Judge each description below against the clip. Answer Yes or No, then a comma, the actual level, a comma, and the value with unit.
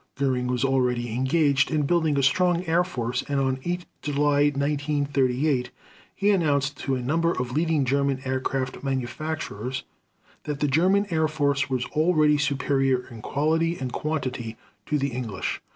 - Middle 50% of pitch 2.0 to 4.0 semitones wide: Yes, average, 3.1 semitones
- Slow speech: No, average, 150 wpm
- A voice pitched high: No, medium, 140 Hz